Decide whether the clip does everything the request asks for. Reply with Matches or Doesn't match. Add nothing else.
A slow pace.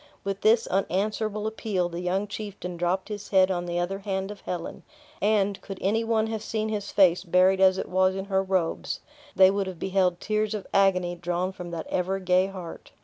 Doesn't match